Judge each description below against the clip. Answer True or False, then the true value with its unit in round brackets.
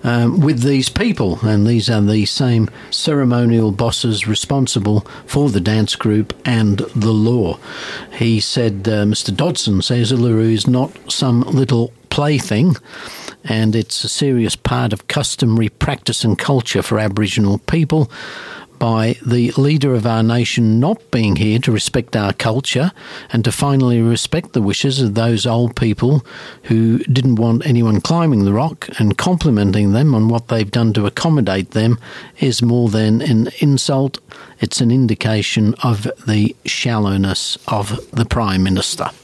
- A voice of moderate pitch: False (115 Hz)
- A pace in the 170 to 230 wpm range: False (150 wpm)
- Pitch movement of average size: True (3.2 semitones)